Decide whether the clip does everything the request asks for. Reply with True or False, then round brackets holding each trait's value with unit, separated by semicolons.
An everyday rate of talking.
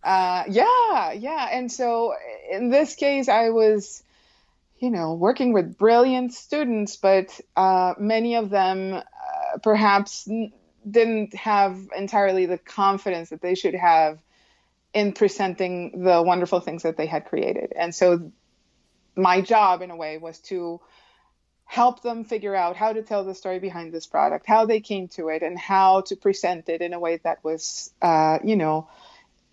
True (165 wpm)